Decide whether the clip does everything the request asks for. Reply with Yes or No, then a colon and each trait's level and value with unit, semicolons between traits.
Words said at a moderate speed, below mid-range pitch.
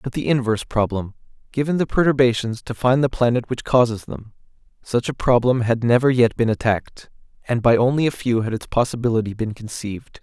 Yes: average, 180 wpm; low, 120 Hz